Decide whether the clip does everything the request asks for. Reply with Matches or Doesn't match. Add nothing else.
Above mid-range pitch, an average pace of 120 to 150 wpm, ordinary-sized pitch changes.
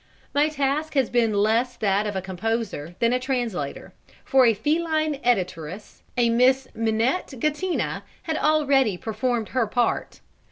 Matches